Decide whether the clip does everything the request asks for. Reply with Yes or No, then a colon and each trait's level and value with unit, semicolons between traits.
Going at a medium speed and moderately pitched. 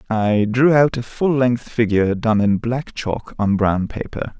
No: average, 190 wpm; low, 115 Hz